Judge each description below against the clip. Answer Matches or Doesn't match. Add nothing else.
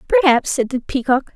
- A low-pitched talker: Doesn't match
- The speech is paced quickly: Doesn't match